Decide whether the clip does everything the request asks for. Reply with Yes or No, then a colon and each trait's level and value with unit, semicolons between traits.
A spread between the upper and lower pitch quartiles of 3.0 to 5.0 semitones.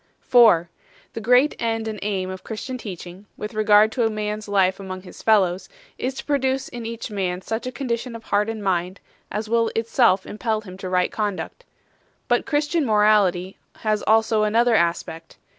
Yes: average, 3.4 semitones